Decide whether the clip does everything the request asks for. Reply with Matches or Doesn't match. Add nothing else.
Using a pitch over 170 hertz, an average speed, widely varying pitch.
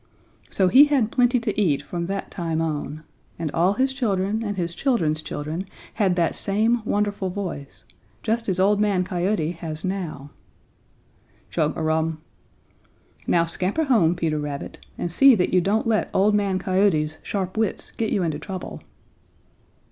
Doesn't match